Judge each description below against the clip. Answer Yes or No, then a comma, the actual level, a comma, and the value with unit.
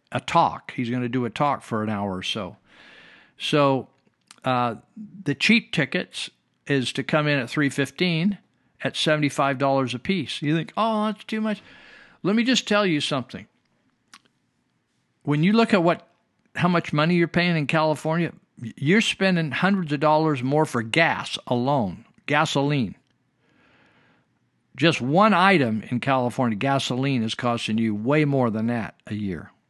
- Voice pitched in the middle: Yes, medium, 145 Hz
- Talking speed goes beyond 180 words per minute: No, average, 160 wpm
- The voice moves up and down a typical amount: No, wide, 5.7 semitones